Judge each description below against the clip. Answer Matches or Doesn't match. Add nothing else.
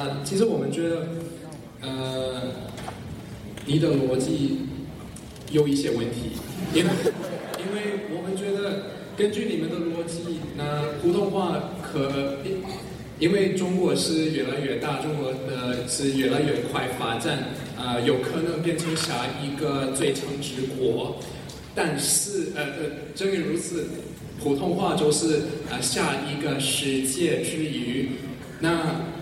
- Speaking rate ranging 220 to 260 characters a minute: Doesn't match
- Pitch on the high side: Doesn't match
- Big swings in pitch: Doesn't match